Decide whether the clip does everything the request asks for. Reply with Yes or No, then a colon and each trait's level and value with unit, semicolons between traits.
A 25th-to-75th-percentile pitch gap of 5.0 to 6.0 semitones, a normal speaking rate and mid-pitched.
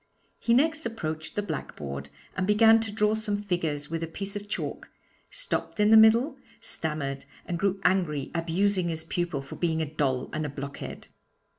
Yes: average, 5.3 semitones; average, 175 wpm; medium, 175 Hz